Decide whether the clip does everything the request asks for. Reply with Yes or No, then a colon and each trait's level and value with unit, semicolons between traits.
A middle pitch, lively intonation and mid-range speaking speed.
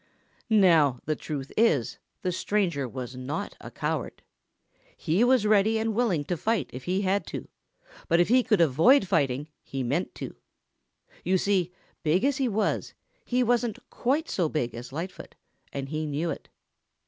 Yes: medium, 180 Hz; wide, 7.0 semitones; average, 165 wpm